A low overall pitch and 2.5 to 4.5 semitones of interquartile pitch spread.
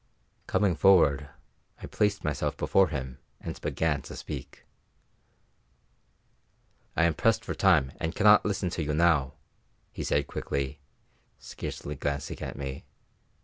No: very low, 80 Hz; average, 5.2 semitones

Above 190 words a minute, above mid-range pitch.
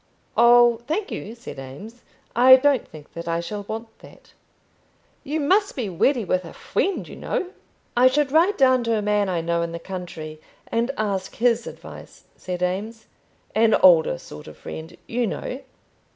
No: average, 175 wpm; high, 220 Hz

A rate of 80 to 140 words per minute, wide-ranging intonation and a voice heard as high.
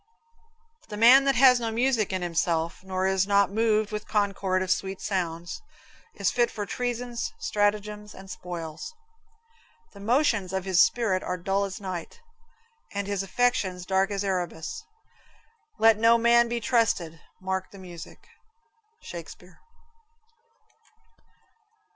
No: slow, 135 wpm; average, 3.6 semitones; high, 200 Hz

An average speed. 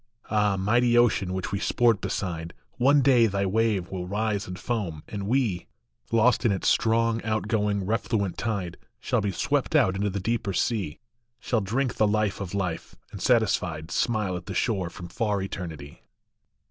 Yes: average, 170 wpm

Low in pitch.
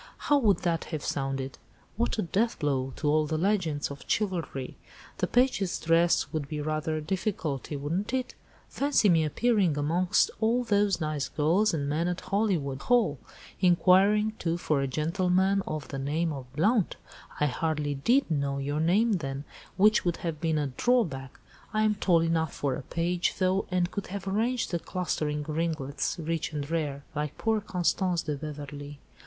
No: medium, 165 Hz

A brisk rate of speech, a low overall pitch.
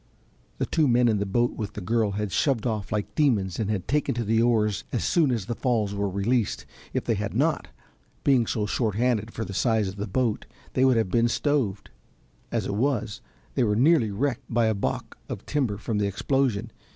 Yes: fast, 210 wpm; low, 115 Hz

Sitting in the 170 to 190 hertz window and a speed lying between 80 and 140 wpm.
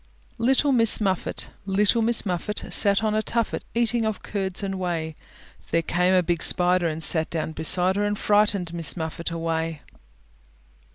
No: medium, 185 Hz; average, 165 wpm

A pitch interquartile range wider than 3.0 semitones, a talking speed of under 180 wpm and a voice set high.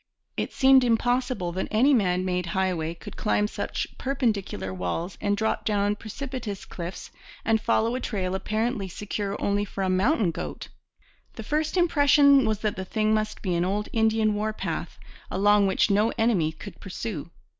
Yes: average, 3.4 semitones; average, 165 wpm; high, 210 Hz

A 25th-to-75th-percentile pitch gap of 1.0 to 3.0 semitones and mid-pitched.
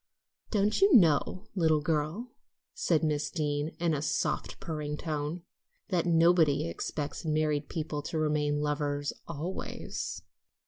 Yes: narrow, 2.4 semitones; medium, 155 Hz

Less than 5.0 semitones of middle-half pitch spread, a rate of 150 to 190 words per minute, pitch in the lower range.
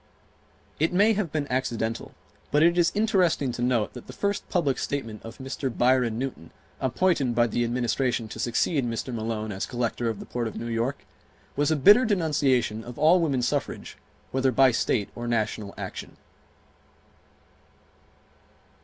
Yes: average, 4.4 semitones; average, 160 wpm; low, 125 Hz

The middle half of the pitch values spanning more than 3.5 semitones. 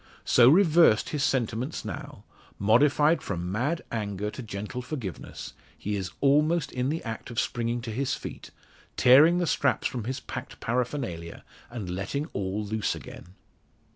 Yes: wide, 5.4 semitones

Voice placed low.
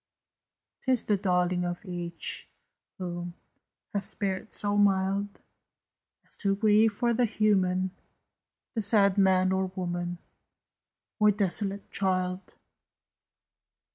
No: high, 195 Hz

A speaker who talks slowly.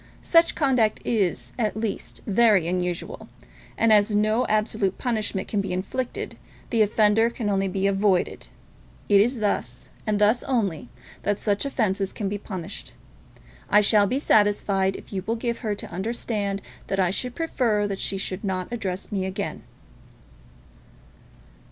No: average, 150 wpm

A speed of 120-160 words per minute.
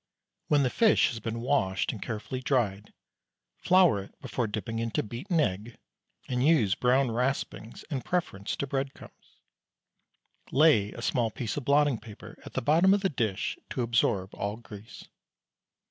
Yes: average, 155 wpm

